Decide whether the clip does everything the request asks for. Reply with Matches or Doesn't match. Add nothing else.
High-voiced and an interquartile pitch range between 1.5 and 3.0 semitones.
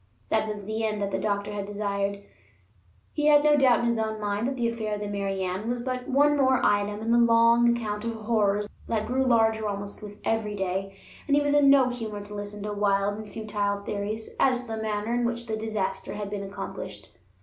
Matches